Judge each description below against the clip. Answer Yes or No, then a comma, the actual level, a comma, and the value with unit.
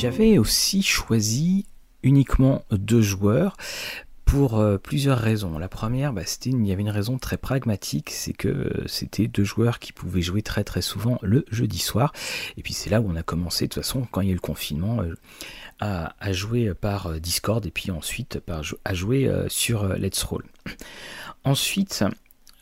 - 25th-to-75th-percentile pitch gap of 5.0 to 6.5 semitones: Yes, average, 5.3 semitones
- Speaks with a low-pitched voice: Yes, low, 105 Hz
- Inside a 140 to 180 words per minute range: No, average, 195 wpm